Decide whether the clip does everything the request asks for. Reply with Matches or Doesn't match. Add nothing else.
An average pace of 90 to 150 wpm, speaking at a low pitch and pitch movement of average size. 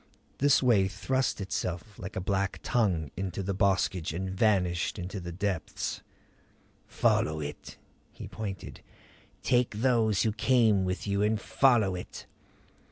Matches